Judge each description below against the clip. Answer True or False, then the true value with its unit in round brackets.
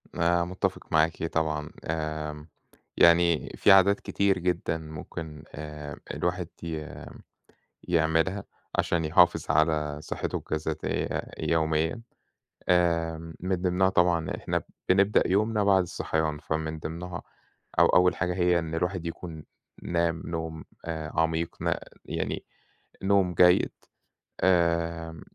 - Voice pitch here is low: True (85 Hz)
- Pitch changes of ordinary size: False (2.0 semitones)